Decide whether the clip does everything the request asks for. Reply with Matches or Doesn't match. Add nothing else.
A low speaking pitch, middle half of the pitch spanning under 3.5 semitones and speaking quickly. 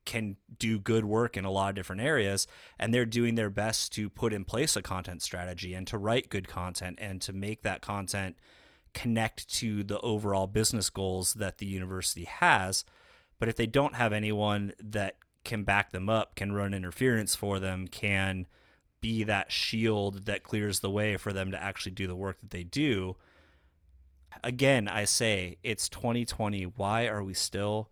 Doesn't match